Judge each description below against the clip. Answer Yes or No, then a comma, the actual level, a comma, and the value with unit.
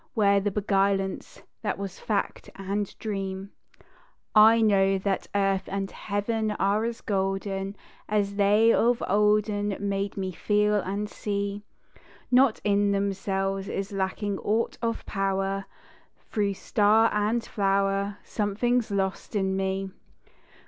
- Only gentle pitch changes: Yes, narrow, 1.3 semitones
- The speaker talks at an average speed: No, slow, 120 wpm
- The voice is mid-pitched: No, high, 200 Hz